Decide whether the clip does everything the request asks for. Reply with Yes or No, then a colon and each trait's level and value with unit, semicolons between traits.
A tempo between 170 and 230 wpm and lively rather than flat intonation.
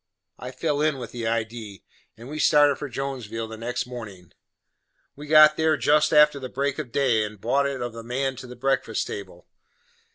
No: average, 195 wpm; average, 4.0 semitones